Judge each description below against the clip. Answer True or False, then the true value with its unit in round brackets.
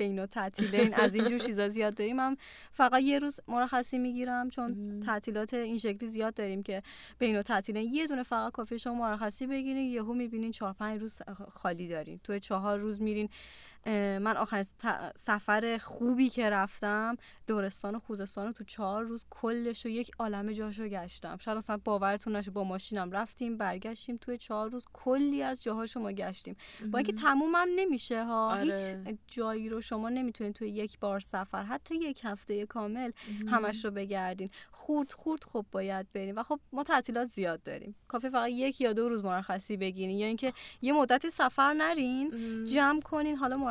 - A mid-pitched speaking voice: False (225 Hz)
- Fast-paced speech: True (180 wpm)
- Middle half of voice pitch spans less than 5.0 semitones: True (3.1 semitones)